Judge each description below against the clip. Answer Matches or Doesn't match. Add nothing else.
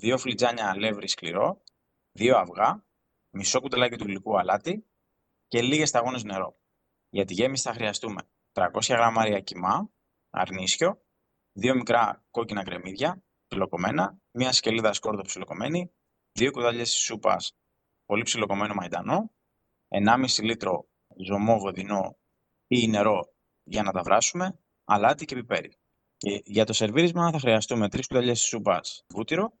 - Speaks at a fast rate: Doesn't match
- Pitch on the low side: Matches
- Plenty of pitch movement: Doesn't match